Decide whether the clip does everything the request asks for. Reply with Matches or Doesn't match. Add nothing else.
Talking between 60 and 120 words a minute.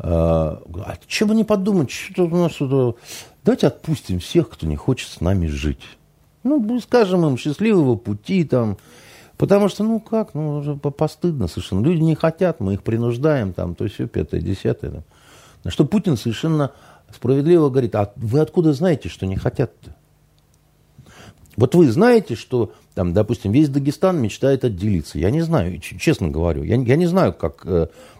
Doesn't match